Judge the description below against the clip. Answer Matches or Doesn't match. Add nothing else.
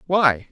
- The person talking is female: Doesn't match